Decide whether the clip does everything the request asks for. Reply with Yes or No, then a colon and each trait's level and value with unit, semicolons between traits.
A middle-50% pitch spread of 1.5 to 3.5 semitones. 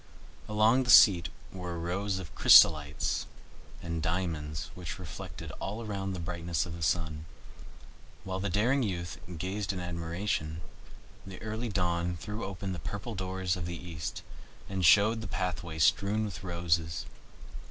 Yes: average, 2.9 semitones